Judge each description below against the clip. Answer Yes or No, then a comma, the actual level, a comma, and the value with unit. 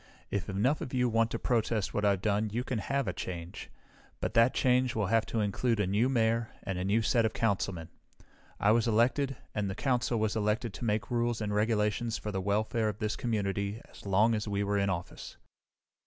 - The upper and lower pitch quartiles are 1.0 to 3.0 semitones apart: Yes, narrow, 2.6 semitones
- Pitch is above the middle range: No, low, 110 Hz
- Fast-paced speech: Yes, fast, 215 wpm